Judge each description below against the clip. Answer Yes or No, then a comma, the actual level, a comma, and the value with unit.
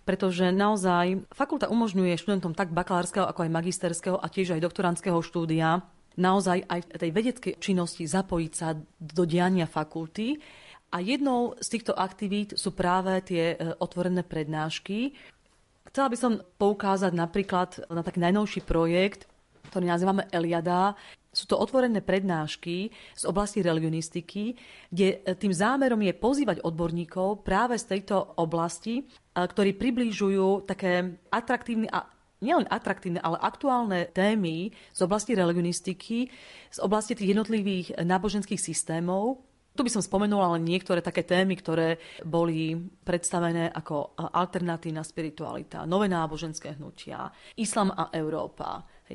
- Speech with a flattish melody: No, average, 3.2 semitones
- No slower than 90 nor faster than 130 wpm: Yes, average, 125 wpm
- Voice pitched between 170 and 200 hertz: Yes, medium, 185 Hz